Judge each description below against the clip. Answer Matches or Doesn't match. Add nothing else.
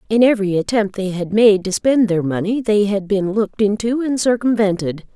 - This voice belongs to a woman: Matches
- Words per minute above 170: Matches